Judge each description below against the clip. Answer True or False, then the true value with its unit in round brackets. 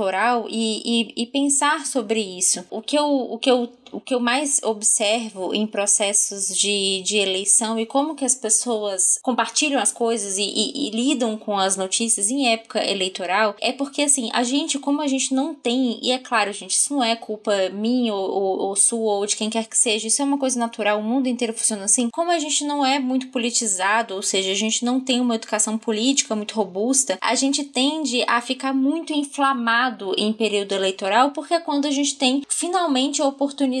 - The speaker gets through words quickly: True (210 wpm)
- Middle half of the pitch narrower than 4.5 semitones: True (4.1 semitones)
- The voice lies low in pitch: False (235 Hz)